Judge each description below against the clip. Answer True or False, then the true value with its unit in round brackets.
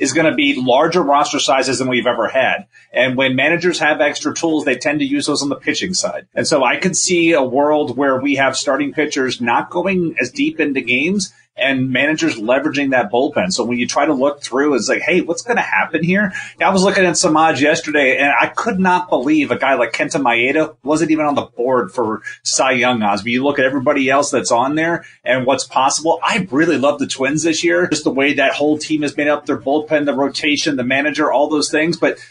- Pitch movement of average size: True (4.4 semitones)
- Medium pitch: True (150 Hz)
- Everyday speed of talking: False (235 wpm)